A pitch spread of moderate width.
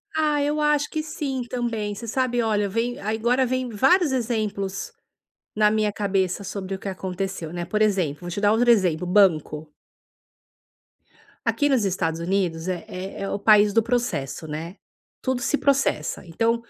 Yes: average, 4.7 semitones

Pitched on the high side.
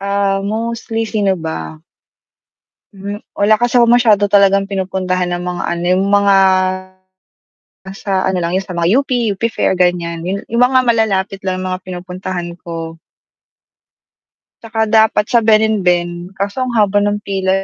Yes: high, 195 Hz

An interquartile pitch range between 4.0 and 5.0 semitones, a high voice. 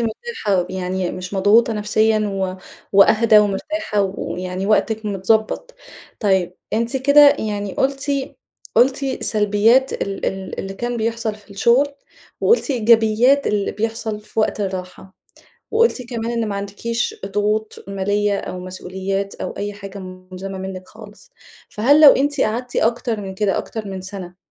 No: average, 3.2 semitones; high, 210 Hz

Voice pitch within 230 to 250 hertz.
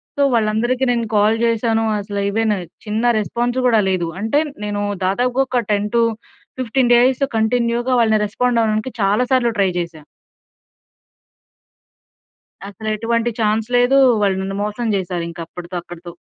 No: high, 220 Hz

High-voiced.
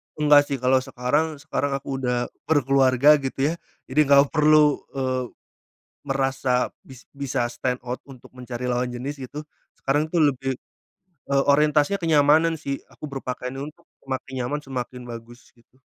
No: low, 135 Hz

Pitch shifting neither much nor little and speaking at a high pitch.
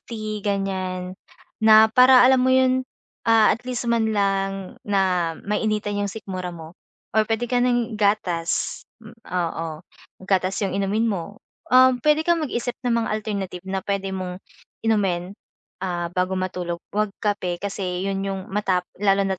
Yes: average, 3.0 semitones; high, 200 Hz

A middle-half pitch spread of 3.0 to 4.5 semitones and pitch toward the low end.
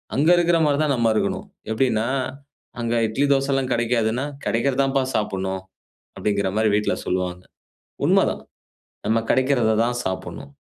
Yes: average, 4.1 semitones; low, 115 Hz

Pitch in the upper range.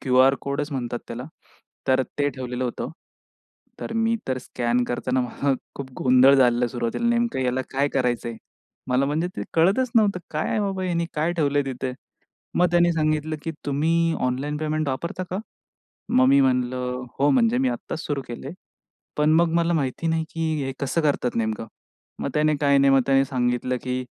No: medium, 140 Hz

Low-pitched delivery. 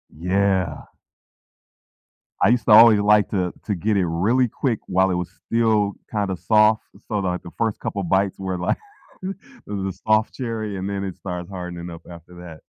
Yes: low, 100 Hz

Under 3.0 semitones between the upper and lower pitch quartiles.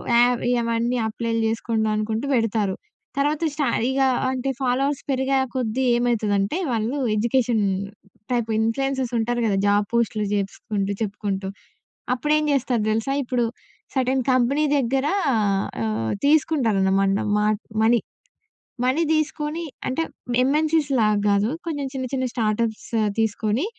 No: average, 3.8 semitones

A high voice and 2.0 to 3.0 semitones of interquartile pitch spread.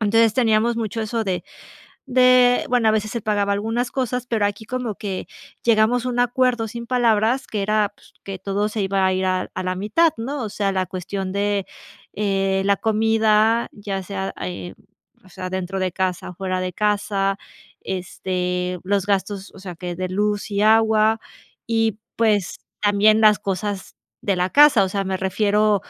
Yes: high, 205 Hz; average, 2.7 semitones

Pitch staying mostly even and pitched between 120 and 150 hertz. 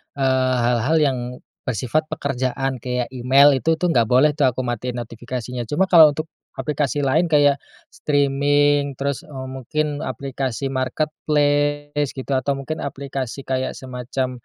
Yes: narrow, 2.3 semitones; low, 135 Hz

